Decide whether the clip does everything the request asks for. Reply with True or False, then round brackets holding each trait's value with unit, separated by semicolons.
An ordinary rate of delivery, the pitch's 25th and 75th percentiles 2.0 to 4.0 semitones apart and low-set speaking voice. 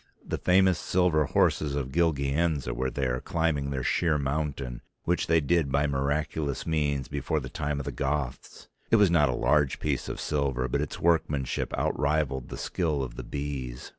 True (175 wpm; 2.7 semitones; 70 Hz)